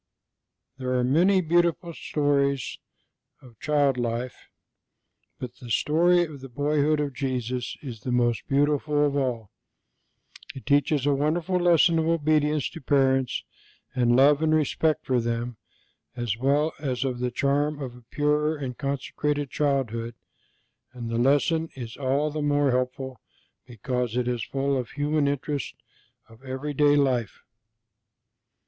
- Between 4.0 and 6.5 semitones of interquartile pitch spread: No, average, 3.0 semitones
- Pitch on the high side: No, medium, 140 Hz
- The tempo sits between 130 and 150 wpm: Yes, average, 140 wpm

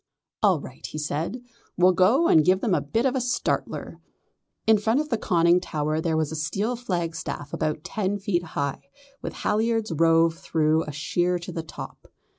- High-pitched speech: No, medium, 175 Hz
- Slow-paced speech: No, average, 185 wpm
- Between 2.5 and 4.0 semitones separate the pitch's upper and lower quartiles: No, average, 5.1 semitones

